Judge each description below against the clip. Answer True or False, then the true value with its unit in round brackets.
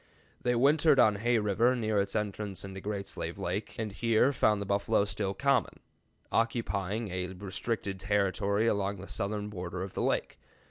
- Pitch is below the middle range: True (105 Hz)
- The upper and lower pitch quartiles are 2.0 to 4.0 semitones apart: True (2.6 semitones)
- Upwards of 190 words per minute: False (170 wpm)